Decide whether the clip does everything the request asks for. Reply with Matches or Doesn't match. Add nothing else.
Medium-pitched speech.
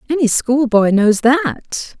Doesn't match